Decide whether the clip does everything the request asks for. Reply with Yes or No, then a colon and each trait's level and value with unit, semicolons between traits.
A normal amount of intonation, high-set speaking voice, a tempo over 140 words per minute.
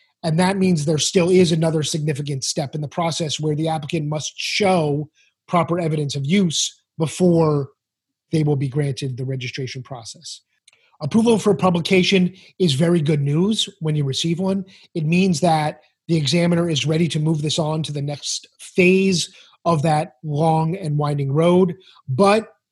No: average, 3.1 semitones; medium, 160 Hz; average, 165 wpm